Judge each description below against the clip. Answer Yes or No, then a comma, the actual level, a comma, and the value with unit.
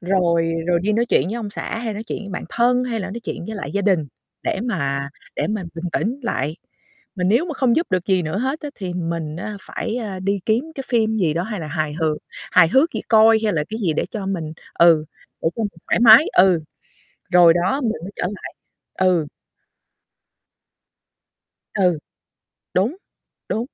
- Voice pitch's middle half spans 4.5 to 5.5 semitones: Yes, average, 4.9 semitones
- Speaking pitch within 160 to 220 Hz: Yes, high, 195 Hz